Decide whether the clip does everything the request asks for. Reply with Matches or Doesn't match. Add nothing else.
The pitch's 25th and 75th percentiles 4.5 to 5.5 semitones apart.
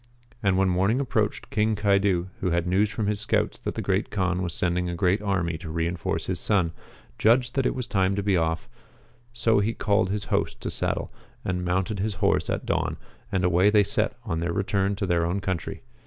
Doesn't match